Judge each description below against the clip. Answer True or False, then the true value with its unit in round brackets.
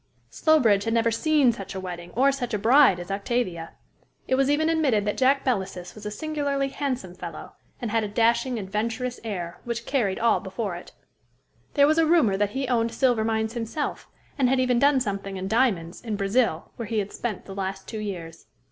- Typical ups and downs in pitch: True (4.9 semitones)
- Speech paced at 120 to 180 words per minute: False (200 wpm)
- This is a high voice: True (225 Hz)